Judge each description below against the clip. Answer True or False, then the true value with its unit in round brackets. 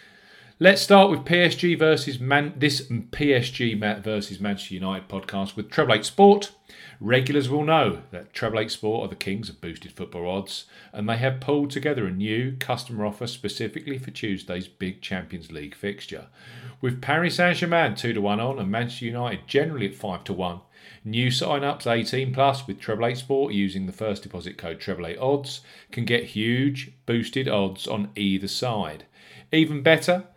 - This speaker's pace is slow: False (160 wpm)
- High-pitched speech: False (120 Hz)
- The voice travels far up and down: True (6.0 semitones)